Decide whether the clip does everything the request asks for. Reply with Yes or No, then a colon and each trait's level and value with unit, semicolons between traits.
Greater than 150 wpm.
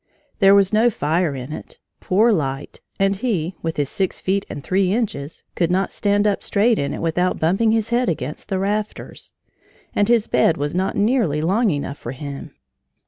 Yes: average, 190 wpm